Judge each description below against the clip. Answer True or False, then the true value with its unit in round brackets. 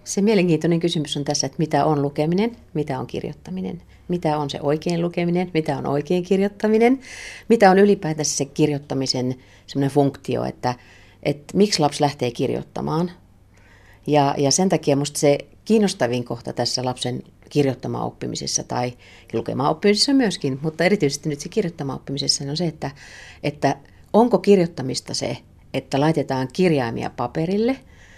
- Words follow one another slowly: False (145 wpm)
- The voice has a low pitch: False (150 Hz)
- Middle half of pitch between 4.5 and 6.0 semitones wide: True (5.0 semitones)